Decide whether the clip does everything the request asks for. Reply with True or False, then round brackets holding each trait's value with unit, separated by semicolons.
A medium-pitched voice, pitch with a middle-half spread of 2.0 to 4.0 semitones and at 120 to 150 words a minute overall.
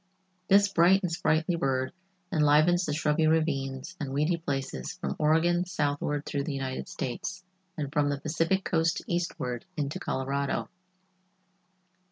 True (150 Hz; 3.3 semitones; 135 wpm)